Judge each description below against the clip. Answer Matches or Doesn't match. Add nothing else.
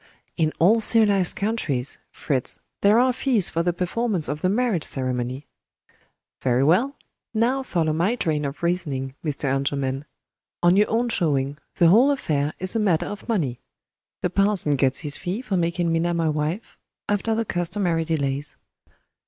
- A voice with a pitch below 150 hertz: Doesn't match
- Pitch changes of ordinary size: Doesn't match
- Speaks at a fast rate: Doesn't match